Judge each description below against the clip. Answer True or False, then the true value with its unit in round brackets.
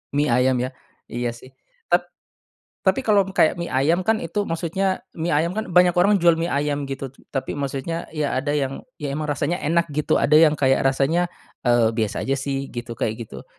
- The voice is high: False (150 Hz)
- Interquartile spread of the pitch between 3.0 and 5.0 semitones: True (4.3 semitones)